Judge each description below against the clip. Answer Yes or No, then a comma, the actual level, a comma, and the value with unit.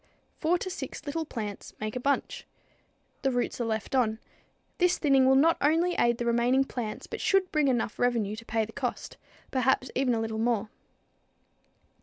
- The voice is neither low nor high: No, very high, 250 Hz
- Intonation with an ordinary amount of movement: Yes, average, 3.9 semitones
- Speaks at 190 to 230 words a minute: No, average, 180 wpm